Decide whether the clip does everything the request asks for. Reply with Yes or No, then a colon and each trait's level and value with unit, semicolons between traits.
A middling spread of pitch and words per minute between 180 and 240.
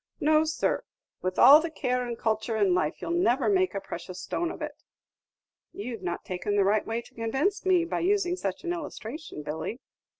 No: wide, 8.9 semitones; average, 200 wpm